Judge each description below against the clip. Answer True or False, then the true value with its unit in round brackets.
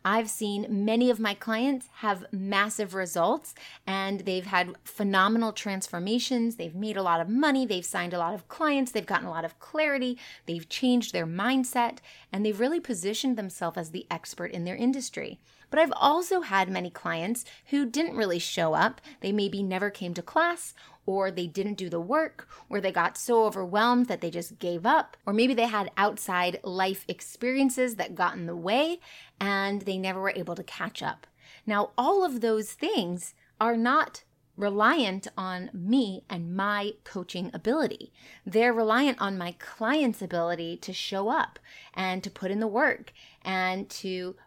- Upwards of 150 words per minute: True (175 wpm)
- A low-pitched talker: False (205 Hz)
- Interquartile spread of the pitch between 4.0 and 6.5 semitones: True (4.6 semitones)